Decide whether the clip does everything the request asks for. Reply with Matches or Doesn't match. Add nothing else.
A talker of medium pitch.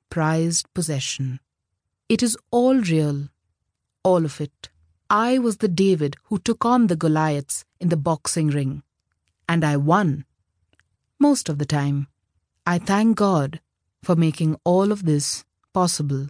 Matches